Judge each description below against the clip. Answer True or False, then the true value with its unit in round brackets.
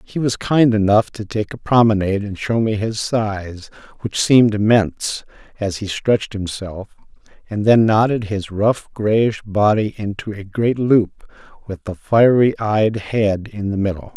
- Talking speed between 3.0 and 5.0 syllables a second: True (4.3 syllables/s)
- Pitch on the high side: False (105 Hz)